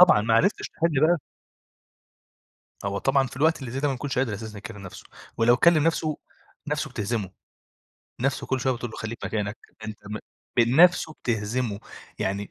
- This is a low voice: Yes, low, 120 Hz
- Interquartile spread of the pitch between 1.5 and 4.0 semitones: No, average, 4.7 semitones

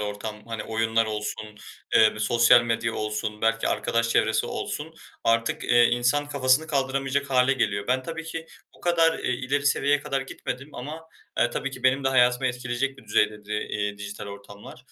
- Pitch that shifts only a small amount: No, average, 4.0 semitones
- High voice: No, low, 120 Hz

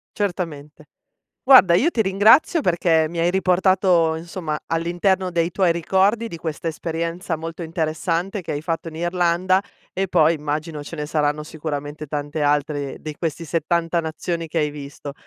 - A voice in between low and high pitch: Yes, medium, 165 Hz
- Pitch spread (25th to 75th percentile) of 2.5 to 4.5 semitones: Yes, average, 2.8 semitones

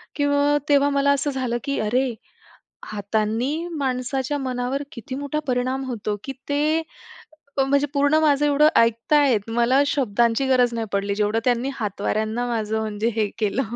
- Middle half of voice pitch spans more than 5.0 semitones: No, average, 3.9 semitones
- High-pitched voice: Yes, very high, 255 Hz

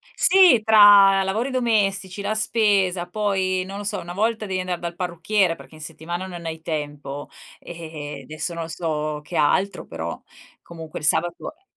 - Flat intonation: No, average, 4.1 semitones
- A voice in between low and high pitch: Yes, medium, 180 Hz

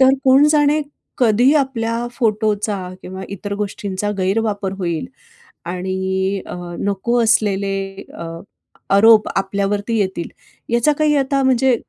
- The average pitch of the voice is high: Yes, high, 210 Hz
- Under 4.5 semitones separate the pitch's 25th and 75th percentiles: Yes, average, 3.8 semitones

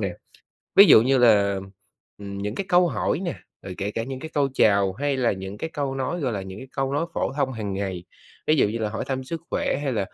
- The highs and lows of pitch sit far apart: Yes, wide, 5.7 semitones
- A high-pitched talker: No, low, 125 Hz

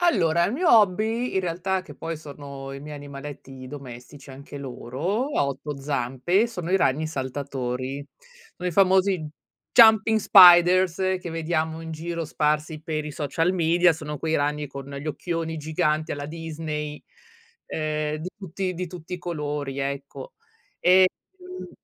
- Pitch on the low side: No, medium, 155 Hz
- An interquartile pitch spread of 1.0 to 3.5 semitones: No, average, 4.0 semitones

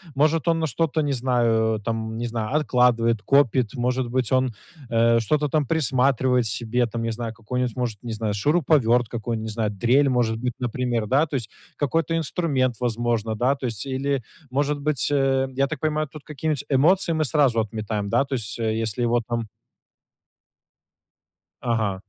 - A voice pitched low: Yes, low, 125 Hz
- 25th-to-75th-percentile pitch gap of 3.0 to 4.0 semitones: Yes, average, 3.6 semitones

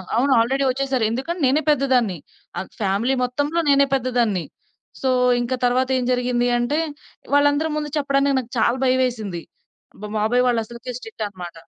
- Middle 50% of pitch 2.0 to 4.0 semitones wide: Yes, average, 2.9 semitones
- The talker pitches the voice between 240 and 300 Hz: Yes, very high, 250 Hz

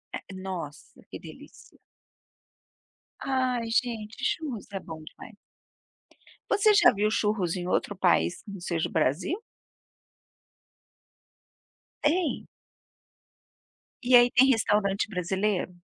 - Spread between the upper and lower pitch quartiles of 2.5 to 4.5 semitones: No, wide, 5.4 semitones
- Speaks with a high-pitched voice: Yes, high, 210 Hz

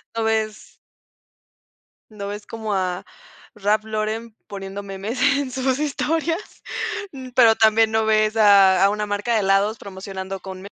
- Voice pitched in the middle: No, high, 215 Hz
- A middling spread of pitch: No, narrow, 2.3 semitones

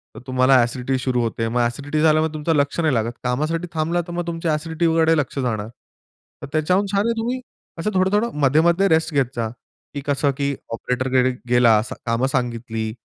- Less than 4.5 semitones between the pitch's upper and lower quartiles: No, average, 4.8 semitones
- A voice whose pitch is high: No, medium, 145 Hz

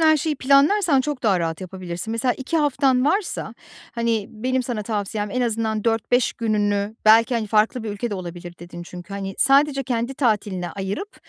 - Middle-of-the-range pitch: No, high, 225 Hz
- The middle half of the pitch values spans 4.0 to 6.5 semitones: Yes, average, 4.7 semitones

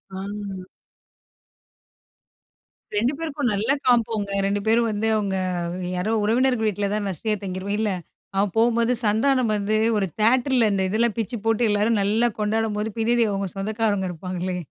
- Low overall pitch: No, high, 215 Hz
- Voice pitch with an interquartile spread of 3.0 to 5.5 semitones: No, narrow, 2.6 semitones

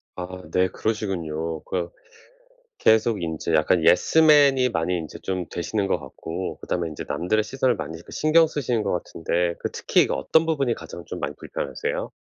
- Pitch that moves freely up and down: Yes, wide, 6.3 semitones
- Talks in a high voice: No, very low, 90 Hz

